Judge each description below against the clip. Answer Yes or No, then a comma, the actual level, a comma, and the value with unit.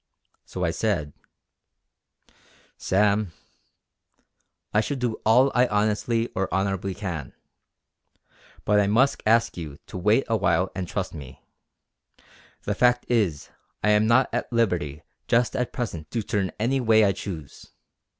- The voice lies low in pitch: Yes, low, 105 Hz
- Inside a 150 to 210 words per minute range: No, average, 140 wpm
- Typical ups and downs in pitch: Yes, average, 4.1 semitones